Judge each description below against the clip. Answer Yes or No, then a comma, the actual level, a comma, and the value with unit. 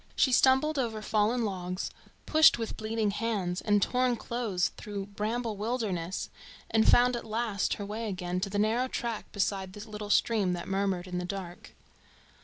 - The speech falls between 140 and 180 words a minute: Yes, average, 170 wpm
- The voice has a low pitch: No, high, 210 Hz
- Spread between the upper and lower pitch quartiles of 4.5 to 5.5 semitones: No, average, 3.2 semitones